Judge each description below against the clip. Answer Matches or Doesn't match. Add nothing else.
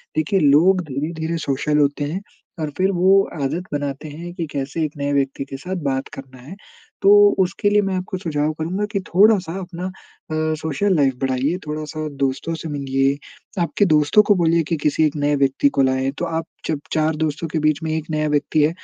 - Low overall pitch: Doesn't match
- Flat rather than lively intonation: Doesn't match